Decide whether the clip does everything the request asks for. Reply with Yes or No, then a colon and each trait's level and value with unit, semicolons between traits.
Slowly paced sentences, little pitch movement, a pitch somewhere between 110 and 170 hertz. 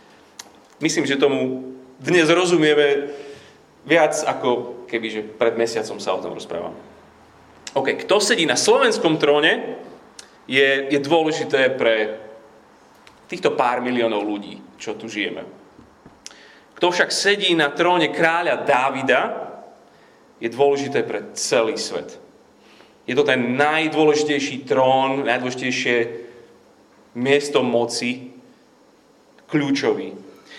No: slow, 105 wpm; average, 3.9 semitones; medium, 140 Hz